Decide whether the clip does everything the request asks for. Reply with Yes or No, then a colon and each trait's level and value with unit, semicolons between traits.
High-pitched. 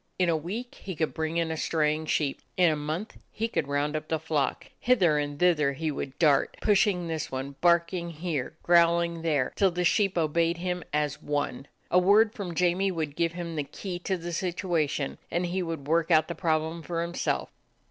No: medium, 165 Hz